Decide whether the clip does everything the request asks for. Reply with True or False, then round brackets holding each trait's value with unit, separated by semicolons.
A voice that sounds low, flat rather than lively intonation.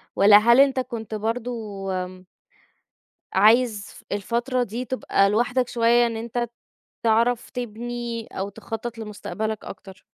False (230 Hz; 2.3 semitones)